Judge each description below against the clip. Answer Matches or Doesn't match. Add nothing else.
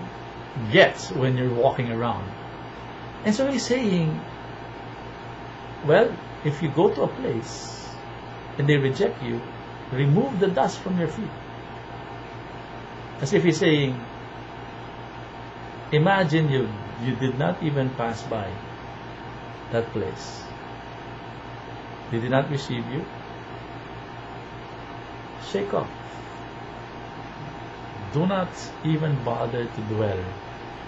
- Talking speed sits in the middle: Doesn't match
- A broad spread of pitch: Doesn't match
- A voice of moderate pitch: Doesn't match